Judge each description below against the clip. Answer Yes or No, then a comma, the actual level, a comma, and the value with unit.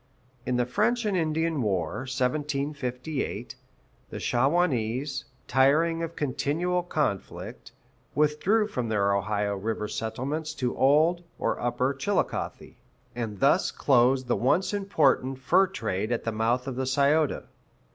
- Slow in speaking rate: Yes, slow, 125 wpm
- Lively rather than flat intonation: No, average, 4.7 semitones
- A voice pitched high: No, low, 135 Hz